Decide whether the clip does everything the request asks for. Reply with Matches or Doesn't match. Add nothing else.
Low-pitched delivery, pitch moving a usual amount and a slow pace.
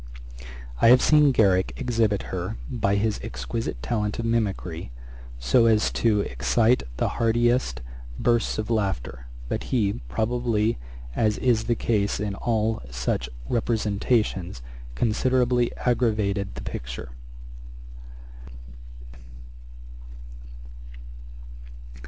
Matches